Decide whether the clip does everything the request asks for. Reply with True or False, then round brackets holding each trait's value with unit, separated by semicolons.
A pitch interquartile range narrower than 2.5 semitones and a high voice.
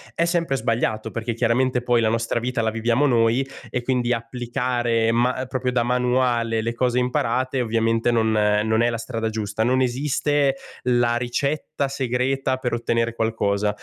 False (1.9 semitones; 120 Hz)